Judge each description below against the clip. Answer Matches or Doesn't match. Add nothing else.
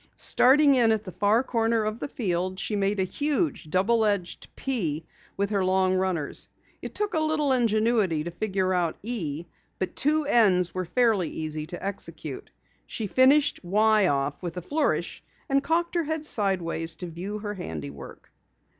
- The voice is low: Doesn't match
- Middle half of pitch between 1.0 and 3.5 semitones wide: Doesn't match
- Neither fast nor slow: Matches